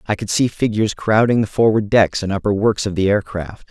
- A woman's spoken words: No, male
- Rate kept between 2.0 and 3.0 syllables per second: No, 5.6 syllables/s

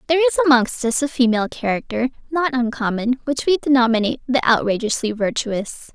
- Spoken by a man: No, female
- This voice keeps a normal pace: Yes, average, 150 wpm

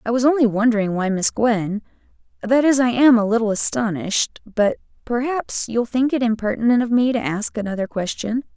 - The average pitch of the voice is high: Yes, high, 230 Hz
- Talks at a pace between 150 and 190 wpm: Yes, average, 160 wpm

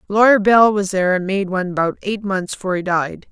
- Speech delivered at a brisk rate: Yes, fast, 235 wpm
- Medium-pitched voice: No, high, 195 Hz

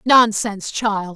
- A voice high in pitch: Yes, high, 215 Hz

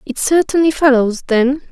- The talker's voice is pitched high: Yes, very high, 275 Hz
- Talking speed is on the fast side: No, average, 140 wpm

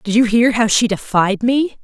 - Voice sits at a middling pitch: No, high, 225 Hz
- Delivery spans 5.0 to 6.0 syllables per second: No, 4.7 syllables/s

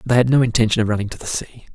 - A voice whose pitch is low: Yes, low, 115 Hz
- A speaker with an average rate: No, fast, 345 wpm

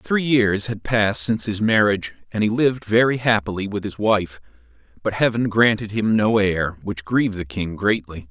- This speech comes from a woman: No, male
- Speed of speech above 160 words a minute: Yes, average, 190 wpm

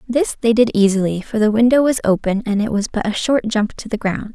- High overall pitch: Yes, high, 220 Hz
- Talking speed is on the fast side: Yes, fast, 260 wpm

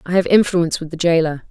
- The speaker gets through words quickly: Yes, fast, 240 wpm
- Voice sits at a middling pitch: Yes, medium, 170 Hz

